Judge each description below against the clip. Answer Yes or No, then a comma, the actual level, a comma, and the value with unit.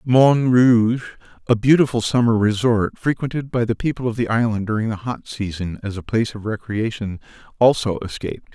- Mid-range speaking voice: No, low, 115 Hz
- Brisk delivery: No, average, 170 wpm